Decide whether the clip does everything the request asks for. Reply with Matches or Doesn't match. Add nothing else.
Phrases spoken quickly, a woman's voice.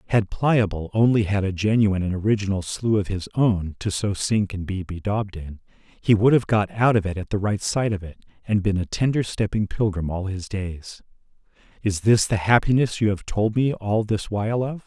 Doesn't match